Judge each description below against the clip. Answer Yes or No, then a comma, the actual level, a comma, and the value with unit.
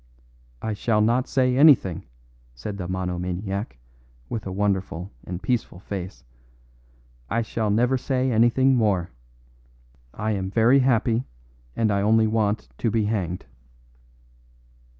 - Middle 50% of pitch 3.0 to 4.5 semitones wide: Yes, average, 3.7 semitones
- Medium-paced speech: No, slow, 125 wpm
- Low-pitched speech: Yes, low, 110 Hz